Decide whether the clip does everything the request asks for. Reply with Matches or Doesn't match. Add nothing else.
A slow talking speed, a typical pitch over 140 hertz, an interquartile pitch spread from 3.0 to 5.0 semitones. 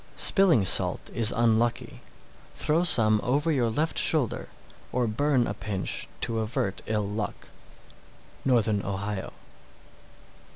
Doesn't match